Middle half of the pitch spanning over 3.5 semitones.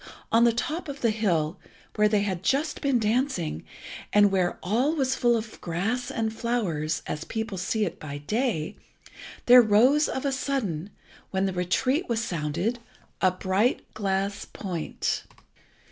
Yes: average, 5.1 semitones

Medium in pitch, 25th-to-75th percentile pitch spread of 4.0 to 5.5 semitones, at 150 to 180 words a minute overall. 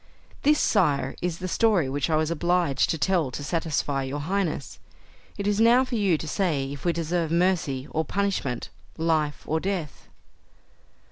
Yes: medium, 165 Hz; average, 4.6 semitones; average, 165 wpm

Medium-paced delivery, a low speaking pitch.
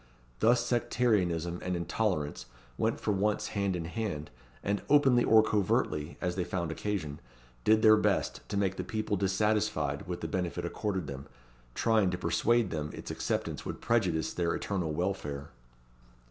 Yes: average, 155 wpm; very low, 95 Hz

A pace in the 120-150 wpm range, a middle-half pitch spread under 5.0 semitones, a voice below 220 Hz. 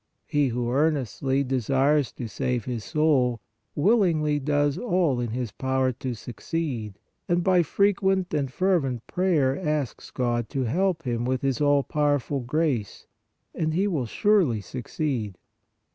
Yes: average, 145 wpm; average, 4.4 semitones; medium, 140 Hz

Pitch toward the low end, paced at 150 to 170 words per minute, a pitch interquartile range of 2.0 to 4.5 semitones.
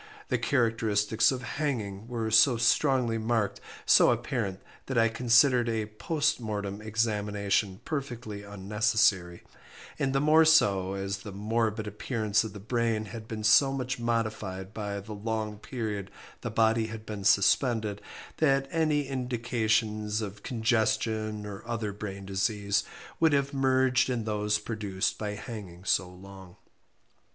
No: low, 110 Hz; average, 140 wpm; average, 2.8 semitones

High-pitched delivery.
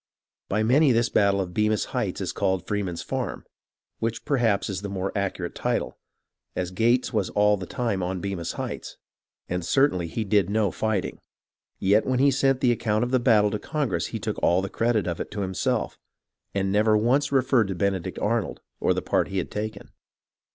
No: low, 105 Hz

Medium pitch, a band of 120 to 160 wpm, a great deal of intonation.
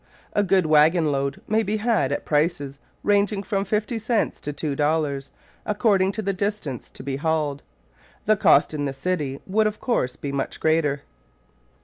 No: medium, 160 Hz; average, 170 wpm; wide, 6.4 semitones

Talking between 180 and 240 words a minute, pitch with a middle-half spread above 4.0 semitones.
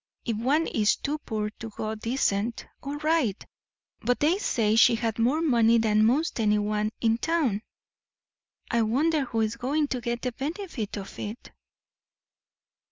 No: average, 155 wpm; average, 4.8 semitones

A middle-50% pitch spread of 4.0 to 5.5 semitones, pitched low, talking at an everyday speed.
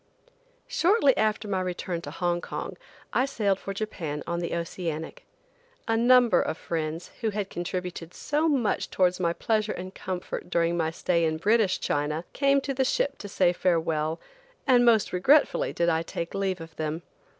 No: average, 4.9 semitones; medium, 185 Hz; average, 170 wpm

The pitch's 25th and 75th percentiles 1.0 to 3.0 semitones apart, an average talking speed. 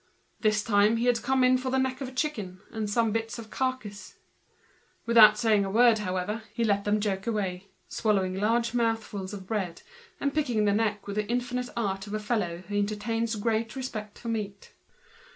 Yes: narrow, 2.5 semitones; average, 190 wpm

